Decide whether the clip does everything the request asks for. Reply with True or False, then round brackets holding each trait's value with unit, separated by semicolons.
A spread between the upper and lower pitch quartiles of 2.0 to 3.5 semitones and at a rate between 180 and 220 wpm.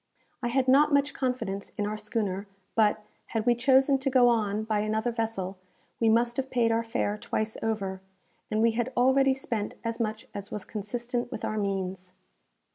True (2.8 semitones; 185 wpm)